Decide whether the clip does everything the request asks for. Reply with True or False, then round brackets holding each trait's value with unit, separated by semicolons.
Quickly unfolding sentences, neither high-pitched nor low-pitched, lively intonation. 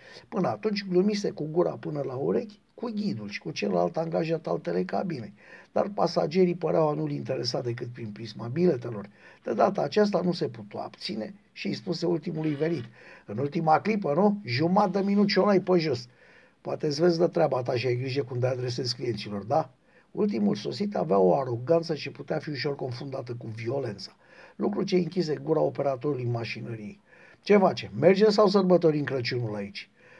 True (175 wpm; 155 Hz; 6.6 semitones)